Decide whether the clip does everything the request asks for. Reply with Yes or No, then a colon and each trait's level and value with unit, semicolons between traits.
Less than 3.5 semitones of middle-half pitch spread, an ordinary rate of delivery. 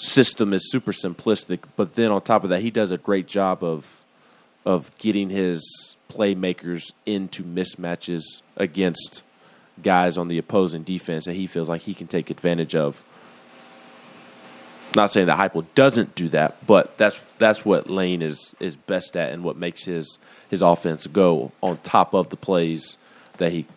Yes: average, 2.8 semitones; average, 175 wpm